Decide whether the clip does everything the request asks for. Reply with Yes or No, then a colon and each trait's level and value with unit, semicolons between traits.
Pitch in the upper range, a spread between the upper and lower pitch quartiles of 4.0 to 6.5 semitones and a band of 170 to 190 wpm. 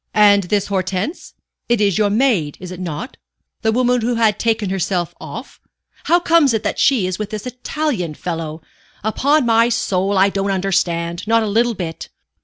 Yes: high, 205 Hz; average, 4.3 semitones; average, 180 wpm